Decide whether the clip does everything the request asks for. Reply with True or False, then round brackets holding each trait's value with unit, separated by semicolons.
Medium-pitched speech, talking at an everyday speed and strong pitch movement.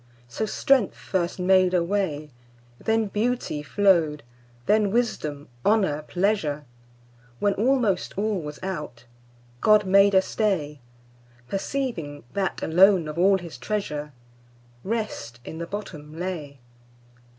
False (170 Hz; 105 wpm; 6.7 semitones)